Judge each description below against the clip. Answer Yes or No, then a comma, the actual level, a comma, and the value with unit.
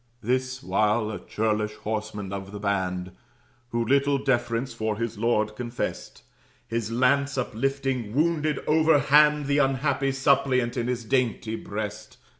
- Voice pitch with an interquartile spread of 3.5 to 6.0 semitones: Yes, average, 4.1 semitones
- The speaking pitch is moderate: No, low, 120 Hz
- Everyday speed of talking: No, slow, 130 wpm